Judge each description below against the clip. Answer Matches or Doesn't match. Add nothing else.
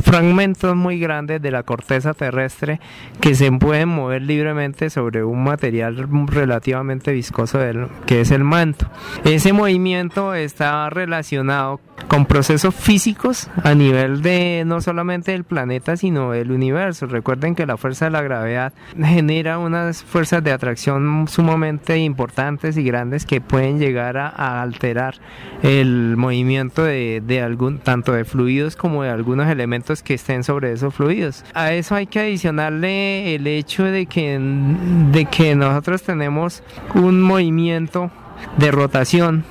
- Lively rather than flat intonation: Doesn't match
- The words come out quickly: Doesn't match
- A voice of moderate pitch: Matches